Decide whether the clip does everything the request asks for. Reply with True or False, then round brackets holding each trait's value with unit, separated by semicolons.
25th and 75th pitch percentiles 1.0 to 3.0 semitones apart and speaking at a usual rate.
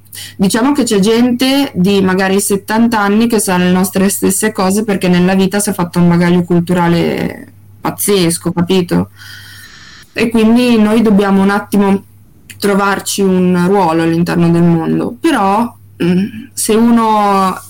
False (3.6 semitones; 135 wpm)